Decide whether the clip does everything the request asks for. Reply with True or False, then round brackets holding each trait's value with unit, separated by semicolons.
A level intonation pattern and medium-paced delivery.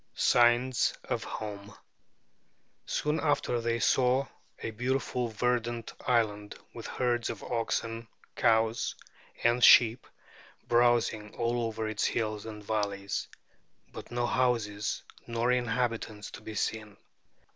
False (2.0 semitones; 115 wpm)